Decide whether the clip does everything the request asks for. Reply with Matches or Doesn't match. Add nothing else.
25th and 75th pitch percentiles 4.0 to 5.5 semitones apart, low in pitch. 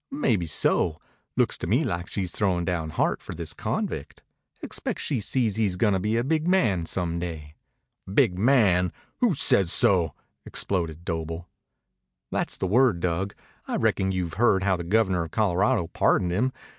Matches